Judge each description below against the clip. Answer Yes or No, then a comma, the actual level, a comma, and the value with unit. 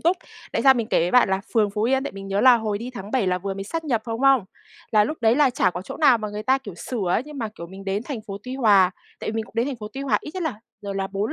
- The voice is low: No, high, 220 Hz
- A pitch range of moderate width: Yes, average, 4.8 semitones